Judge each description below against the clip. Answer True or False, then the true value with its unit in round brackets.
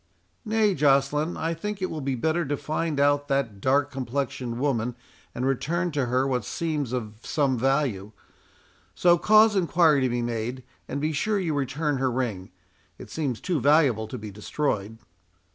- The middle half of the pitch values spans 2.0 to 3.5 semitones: False (4.3 semitones)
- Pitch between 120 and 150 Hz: True (140 Hz)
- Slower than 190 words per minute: True (170 wpm)